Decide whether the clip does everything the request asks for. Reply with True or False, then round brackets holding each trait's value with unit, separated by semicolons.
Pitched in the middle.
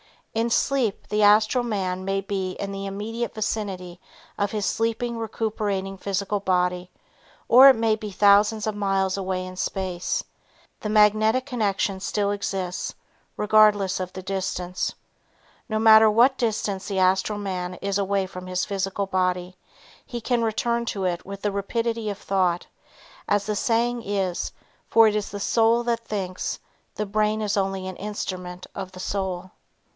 False (200 Hz)